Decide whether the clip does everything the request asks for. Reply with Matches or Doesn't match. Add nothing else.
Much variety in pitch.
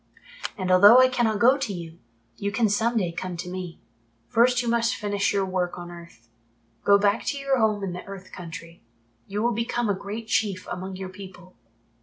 Doesn't match